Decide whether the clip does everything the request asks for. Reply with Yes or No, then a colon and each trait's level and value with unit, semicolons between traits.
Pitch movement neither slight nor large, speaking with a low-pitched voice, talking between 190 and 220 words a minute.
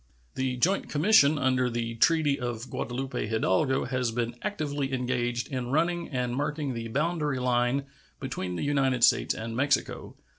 No: average, 3.1 semitones; low, 130 Hz; average, 150 wpm